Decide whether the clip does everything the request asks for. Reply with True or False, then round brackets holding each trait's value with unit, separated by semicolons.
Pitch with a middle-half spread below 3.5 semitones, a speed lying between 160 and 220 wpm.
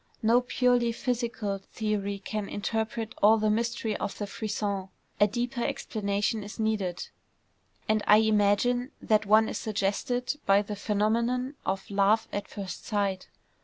False (2.4 semitones; 140 wpm)